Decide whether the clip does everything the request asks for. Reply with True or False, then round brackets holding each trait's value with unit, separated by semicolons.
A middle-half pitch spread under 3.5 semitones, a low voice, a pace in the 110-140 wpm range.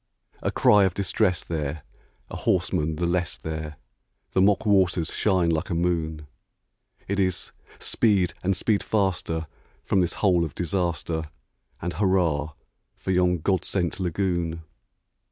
True (2.8 semitones; 90 Hz; 135 wpm)